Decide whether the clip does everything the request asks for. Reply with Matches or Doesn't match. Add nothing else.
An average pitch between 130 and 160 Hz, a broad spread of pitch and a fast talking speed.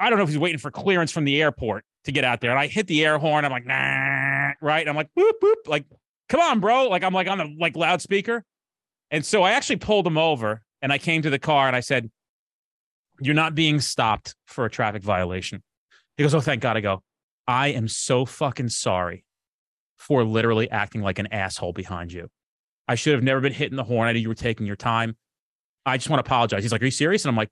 Matches